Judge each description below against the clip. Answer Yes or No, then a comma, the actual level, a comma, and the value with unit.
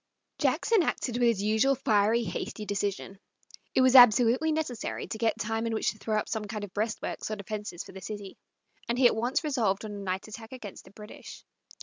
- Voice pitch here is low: No, high, 220 Hz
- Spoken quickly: Yes, fast, 210 wpm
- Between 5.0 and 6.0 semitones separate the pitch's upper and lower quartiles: No, average, 2.8 semitones